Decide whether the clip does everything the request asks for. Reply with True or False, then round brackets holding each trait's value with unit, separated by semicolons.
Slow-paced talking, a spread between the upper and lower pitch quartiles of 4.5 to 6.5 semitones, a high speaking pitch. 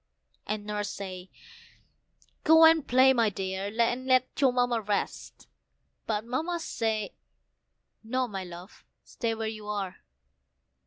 False (125 wpm; 3.9 semitones; 225 Hz)